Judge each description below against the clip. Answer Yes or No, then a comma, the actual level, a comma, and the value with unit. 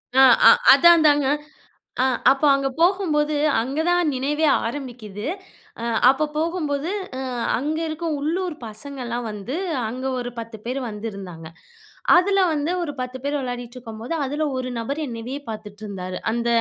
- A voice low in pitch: No, very high, 270 Hz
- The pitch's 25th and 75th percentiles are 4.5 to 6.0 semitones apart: Yes, average, 4.9 semitones